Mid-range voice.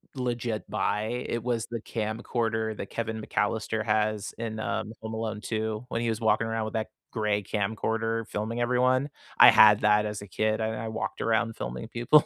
No: low, 110 Hz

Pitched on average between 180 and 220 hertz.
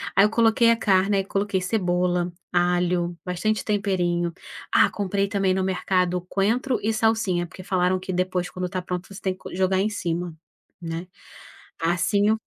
Yes: medium, 185 Hz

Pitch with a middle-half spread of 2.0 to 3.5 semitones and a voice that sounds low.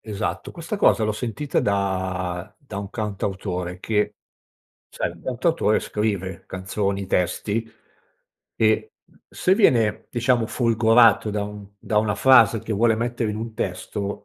Yes: narrow, 2.6 semitones; low, 105 Hz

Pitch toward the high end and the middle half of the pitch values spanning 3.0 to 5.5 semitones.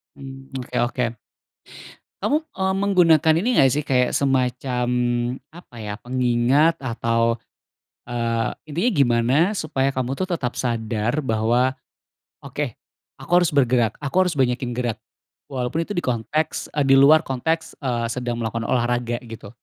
No: low, 125 Hz; average, 4.0 semitones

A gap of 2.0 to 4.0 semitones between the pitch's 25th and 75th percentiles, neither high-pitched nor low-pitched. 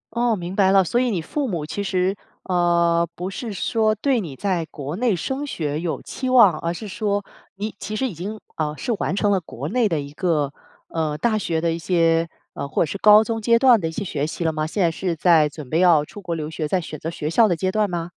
No: average, 4.7 semitones; medium, 180 Hz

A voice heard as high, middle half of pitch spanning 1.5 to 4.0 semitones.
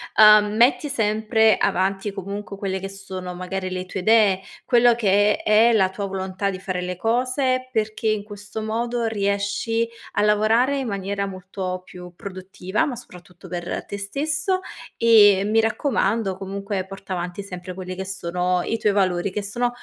Yes: high, 200 Hz; average, 2.9 semitones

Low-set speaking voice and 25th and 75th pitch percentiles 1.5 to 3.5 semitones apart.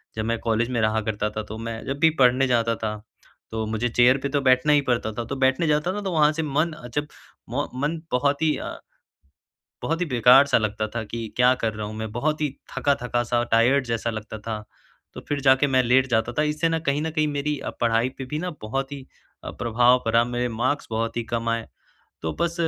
No: low, 125 Hz; average, 4.1 semitones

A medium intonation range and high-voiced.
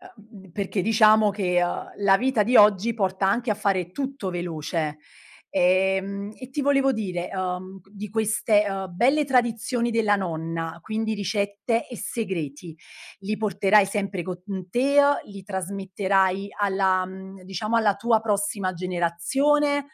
Yes: average, 3.0 semitones; high, 200 Hz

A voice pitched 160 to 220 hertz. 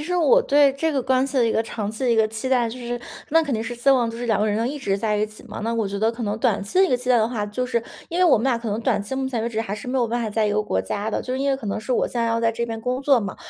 No: high, 235 Hz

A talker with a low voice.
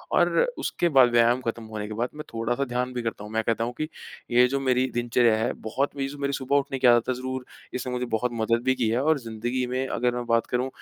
Yes: low, 125 Hz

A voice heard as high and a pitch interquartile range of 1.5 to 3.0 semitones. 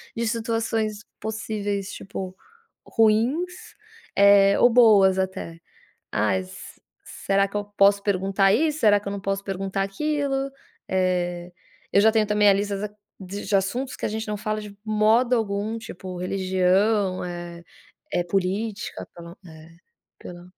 Yes: high, 200 Hz; narrow, 2.6 semitones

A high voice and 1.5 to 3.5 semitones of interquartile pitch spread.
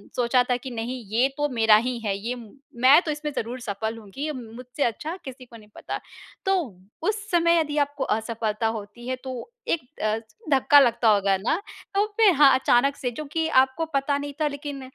No: very high, 255 Hz; average, 4.3 semitones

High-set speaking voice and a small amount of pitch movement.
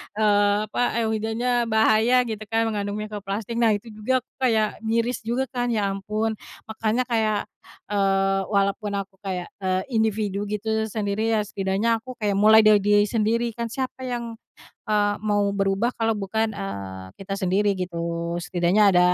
Yes: high, 210 Hz; narrow, 2.2 semitones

